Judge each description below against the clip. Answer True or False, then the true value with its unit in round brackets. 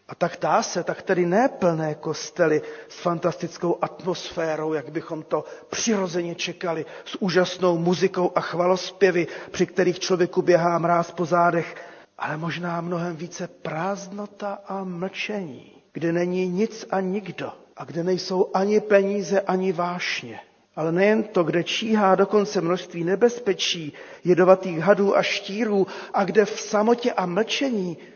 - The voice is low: False (180 Hz)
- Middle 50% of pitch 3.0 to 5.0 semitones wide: False (2.5 semitones)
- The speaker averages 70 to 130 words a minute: False (140 wpm)